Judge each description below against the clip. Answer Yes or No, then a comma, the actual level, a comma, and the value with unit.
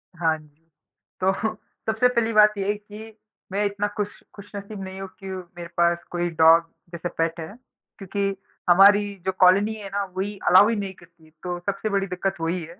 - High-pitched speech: Yes, high, 195 Hz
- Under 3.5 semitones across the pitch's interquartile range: Yes, average, 2.9 semitones